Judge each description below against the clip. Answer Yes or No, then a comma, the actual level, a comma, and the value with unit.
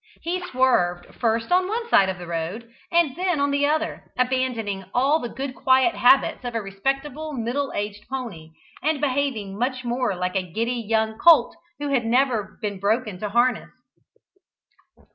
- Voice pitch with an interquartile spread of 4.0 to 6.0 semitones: Yes, average, 5.1 semitones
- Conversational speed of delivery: Yes, average, 165 wpm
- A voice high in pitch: Yes, high, 245 Hz